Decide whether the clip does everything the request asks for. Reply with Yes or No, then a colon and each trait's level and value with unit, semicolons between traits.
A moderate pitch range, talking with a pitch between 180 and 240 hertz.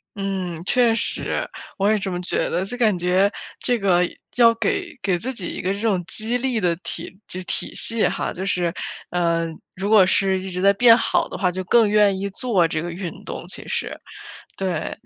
Yes: average, 3.6 semitones; high, 195 Hz